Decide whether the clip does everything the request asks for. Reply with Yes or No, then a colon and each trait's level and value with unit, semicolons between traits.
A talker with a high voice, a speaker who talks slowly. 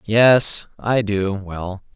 No: low, 105 Hz; slow, 90 wpm